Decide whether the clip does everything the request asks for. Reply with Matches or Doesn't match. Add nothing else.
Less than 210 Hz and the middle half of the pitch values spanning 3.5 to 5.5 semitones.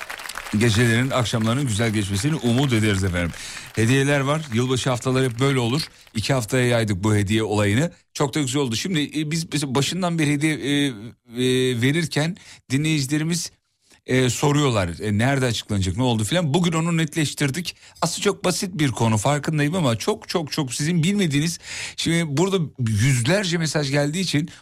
Matches